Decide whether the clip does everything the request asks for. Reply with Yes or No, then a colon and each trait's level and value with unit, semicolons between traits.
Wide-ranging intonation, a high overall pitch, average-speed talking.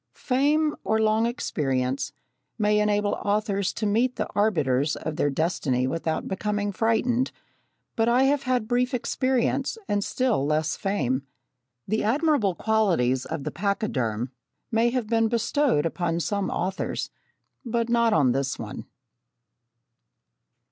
No: wide, 6.9 semitones; high, 210 Hz; slow, 130 wpm